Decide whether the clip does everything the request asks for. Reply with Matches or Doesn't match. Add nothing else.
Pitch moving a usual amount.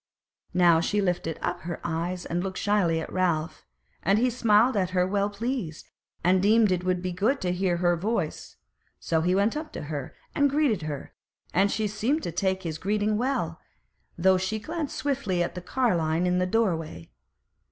Matches